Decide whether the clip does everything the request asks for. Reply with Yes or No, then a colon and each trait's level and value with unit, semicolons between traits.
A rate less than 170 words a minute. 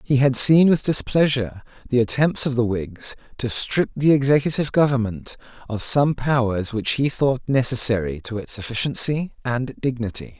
Yes: average, 155 wpm